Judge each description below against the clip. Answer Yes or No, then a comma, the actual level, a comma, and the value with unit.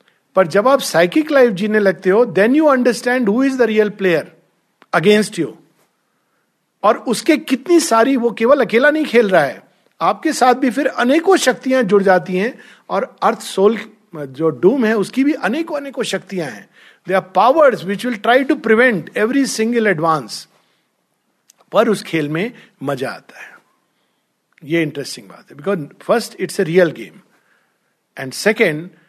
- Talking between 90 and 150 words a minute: No, average, 165 wpm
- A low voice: No, high, 215 Hz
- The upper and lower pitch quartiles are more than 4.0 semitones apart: Yes, wide, 5.5 semitones